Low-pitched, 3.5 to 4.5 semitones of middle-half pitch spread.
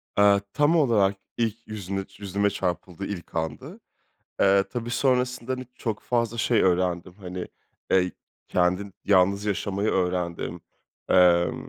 Yes: low, 100 Hz; average, 3.9 semitones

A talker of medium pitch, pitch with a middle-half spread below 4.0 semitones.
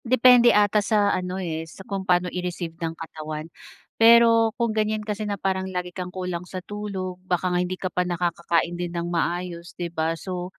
Yes: medium, 180 Hz; average, 3.1 semitones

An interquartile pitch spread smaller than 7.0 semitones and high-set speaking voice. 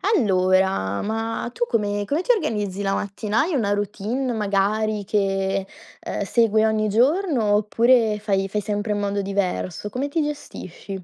Yes: narrow, 2.6 semitones; high, 210 Hz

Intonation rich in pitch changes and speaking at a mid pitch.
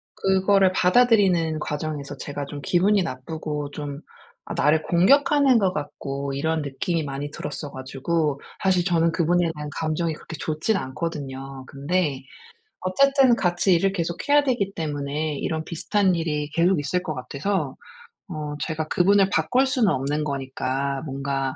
No: average, 4.5 semitones; medium, 160 Hz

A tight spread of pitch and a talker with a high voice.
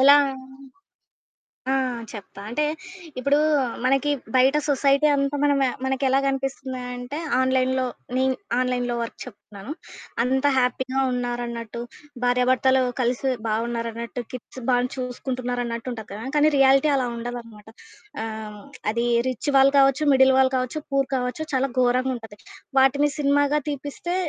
Yes: narrow, 2.0 semitones; very high, 255 Hz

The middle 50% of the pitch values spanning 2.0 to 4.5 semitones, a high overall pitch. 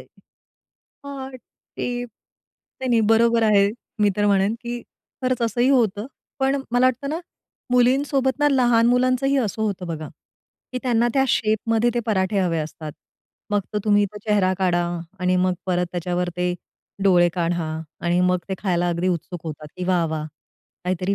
No: average, 5.3 semitones; high, 210 Hz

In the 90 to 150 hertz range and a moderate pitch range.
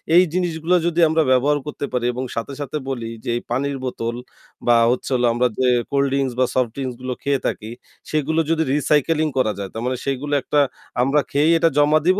Yes: medium, 140 Hz; average, 3.5 semitones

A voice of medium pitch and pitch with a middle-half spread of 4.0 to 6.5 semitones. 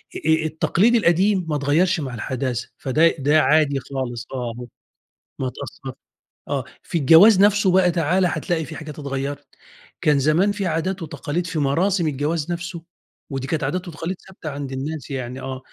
Yes: medium, 155 Hz; average, 4.3 semitones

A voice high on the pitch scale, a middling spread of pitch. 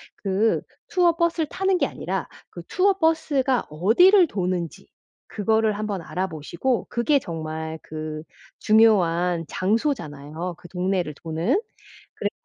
No: high, 195 Hz; wide, 8.8 semitones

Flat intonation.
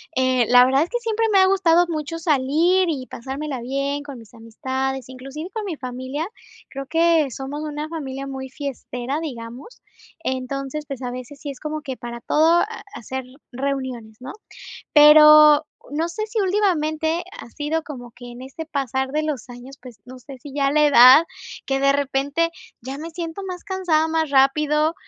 No: average, 3.5 semitones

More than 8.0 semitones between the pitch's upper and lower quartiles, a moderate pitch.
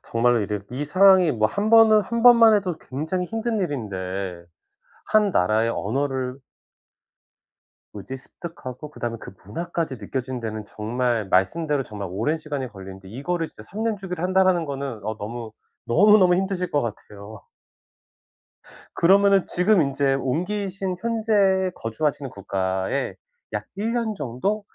Yes: wide, 9.0 semitones; medium, 145 Hz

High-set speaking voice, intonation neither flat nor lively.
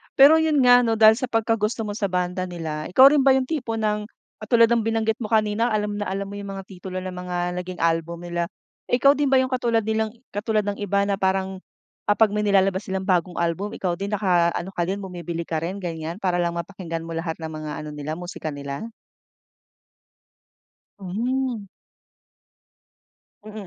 Yes: high, 200 Hz; average, 4.0 semitones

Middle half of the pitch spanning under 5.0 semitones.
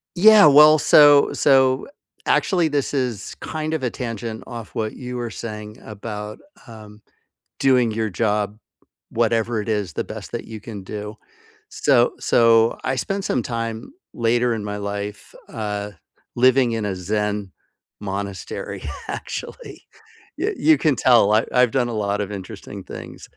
Yes: average, 3.7 semitones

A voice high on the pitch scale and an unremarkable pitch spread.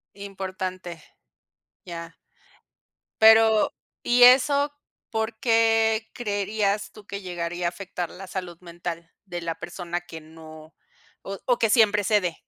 Yes: high, 195 Hz; average, 4.2 semitones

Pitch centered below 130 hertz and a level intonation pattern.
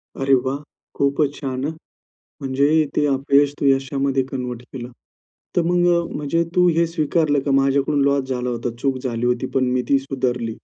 No: low, 135 Hz; narrow, 1.8 semitones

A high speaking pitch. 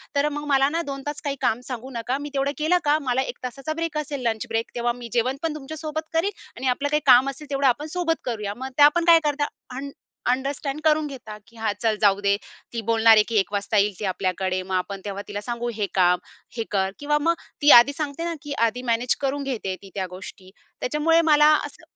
Yes: very high, 265 Hz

